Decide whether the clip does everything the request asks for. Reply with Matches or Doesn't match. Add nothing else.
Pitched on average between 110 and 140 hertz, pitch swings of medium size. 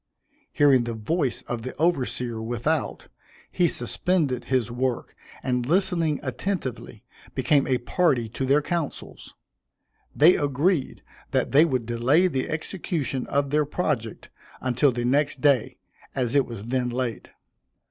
Matches